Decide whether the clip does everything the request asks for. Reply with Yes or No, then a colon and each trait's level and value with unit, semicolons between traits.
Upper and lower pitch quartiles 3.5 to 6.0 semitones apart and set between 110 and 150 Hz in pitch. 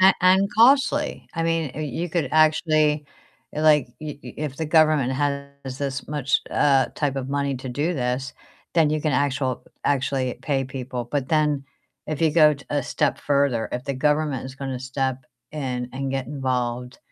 No: average, 2.7 semitones; medium, 140 Hz